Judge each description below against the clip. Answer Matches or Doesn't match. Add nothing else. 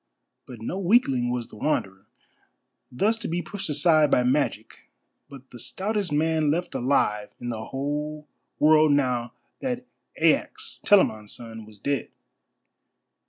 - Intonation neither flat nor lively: Doesn't match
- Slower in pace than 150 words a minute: Matches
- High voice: Doesn't match